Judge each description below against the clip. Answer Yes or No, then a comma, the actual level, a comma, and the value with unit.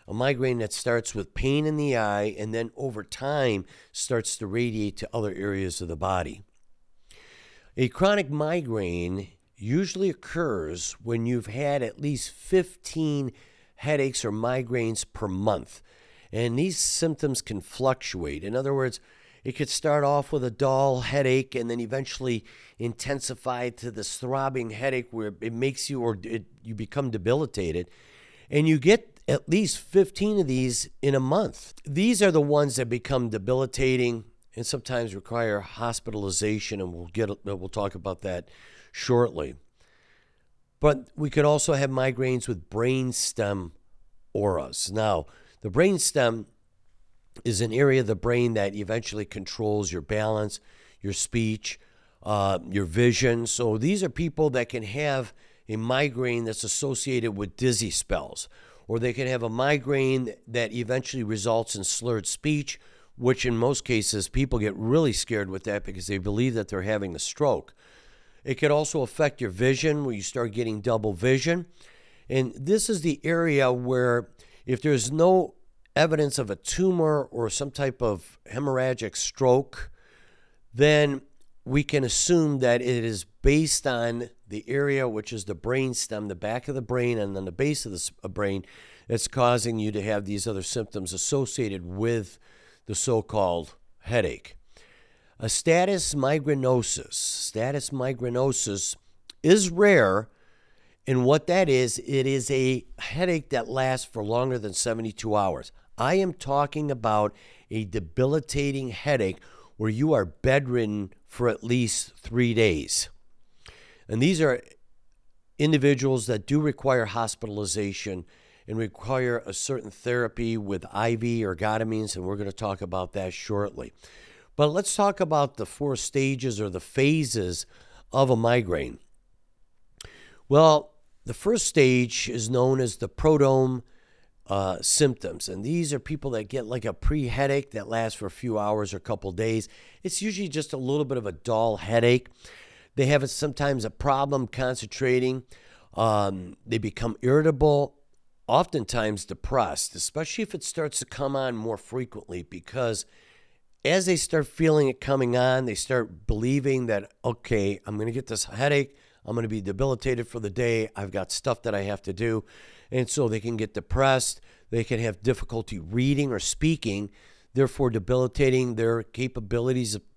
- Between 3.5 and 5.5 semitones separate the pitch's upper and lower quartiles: Yes, average, 4.3 semitones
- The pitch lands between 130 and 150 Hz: No, low, 120 Hz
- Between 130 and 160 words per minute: Yes, average, 155 wpm